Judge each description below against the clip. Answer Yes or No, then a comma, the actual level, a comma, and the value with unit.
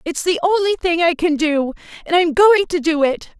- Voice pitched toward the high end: Yes, very high, 335 Hz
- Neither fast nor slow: No, fast, 250 wpm